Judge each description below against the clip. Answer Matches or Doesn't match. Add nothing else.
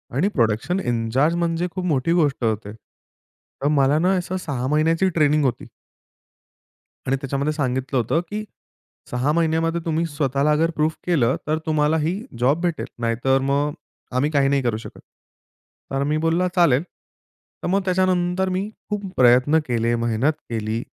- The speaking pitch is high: Doesn't match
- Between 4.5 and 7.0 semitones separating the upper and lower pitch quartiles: Matches